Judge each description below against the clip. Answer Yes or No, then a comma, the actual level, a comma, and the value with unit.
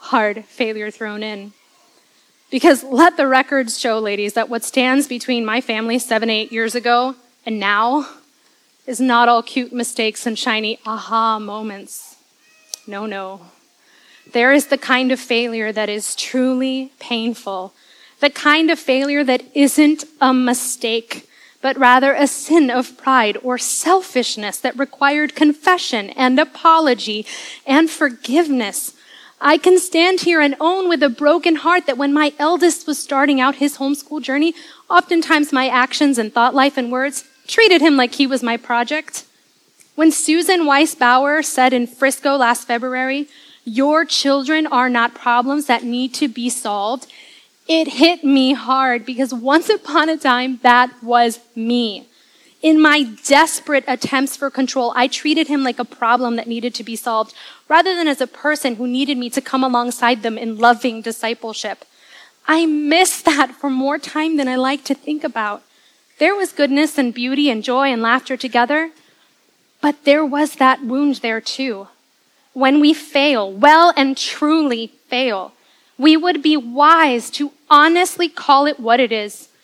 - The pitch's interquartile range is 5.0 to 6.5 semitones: No, average, 3.8 semitones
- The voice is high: Yes, very high, 265 Hz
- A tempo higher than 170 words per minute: No, average, 160 wpm